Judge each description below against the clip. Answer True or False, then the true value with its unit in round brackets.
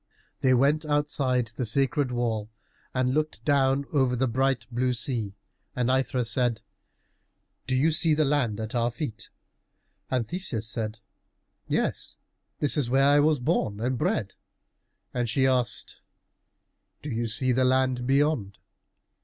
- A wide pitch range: False (3.1 semitones)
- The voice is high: False (130 Hz)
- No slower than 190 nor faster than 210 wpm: False (145 wpm)